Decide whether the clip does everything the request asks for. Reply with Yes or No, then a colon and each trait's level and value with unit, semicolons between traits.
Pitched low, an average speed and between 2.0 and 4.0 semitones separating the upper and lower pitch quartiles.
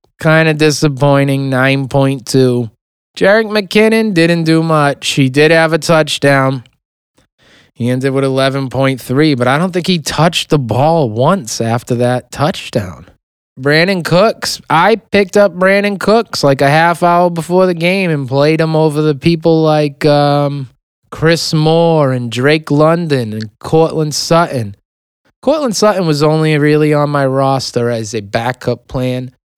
No: medium, 150 Hz; average, 145 wpm; average, 3.7 semitones